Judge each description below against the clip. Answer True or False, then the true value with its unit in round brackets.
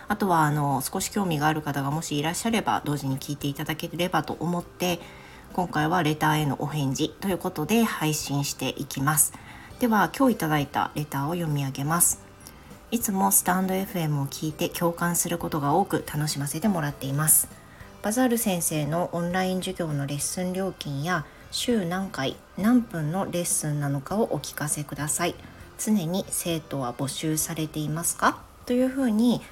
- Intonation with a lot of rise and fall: False (4.2 semitones)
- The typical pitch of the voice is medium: True (160 Hz)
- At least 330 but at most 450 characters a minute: True (370 characters per minute)